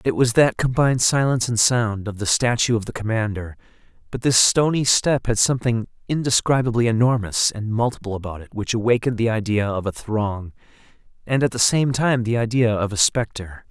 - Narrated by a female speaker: No, male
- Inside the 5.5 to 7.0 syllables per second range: Yes, 5.6 syllables/s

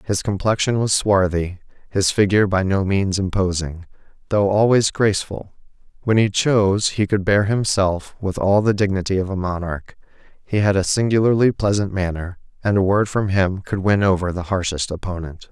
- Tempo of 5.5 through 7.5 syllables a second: No, 5.1 syllables/s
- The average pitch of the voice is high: No, low, 100 Hz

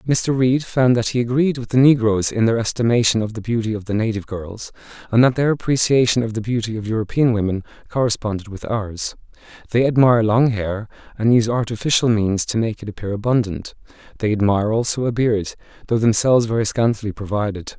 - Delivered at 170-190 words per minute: Yes, average, 185 wpm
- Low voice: Yes, low, 115 Hz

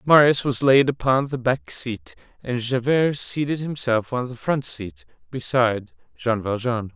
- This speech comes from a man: Yes, male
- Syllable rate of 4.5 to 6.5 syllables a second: No, 4.2 syllables/s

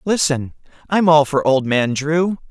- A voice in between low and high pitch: Yes, medium, 155 Hz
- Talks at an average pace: Yes, average, 170 wpm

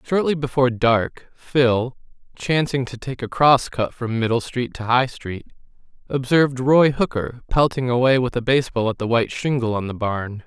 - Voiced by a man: Yes, male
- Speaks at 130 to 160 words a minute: No, average, 180 wpm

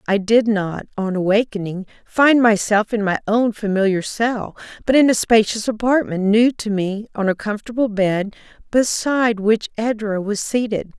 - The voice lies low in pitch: No, high, 215 Hz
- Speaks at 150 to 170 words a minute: Yes, average, 160 wpm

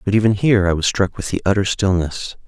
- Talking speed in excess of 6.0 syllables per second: Yes, 6.2 syllables/s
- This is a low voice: Yes, low, 100 Hz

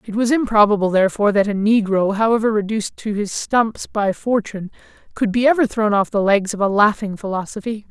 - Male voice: Yes, male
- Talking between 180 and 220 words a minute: Yes, average, 190 wpm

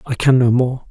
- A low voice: Yes, low, 125 Hz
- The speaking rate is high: Yes, fast, 265 wpm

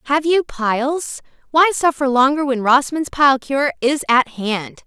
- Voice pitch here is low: No, very high, 275 Hz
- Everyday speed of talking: Yes, average, 160 wpm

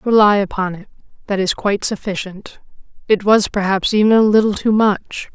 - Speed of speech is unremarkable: Yes, average, 170 wpm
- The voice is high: Yes, high, 200 Hz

